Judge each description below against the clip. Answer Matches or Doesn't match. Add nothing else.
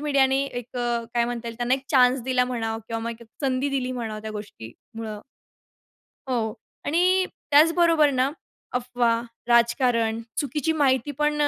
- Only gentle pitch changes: Doesn't match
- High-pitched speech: Matches